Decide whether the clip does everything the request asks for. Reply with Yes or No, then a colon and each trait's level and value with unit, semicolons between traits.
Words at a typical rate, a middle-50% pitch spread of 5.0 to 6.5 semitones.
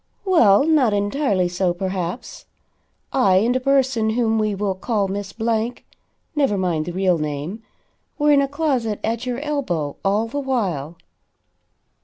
Yes: average, 150 wpm; wide, 5.6 semitones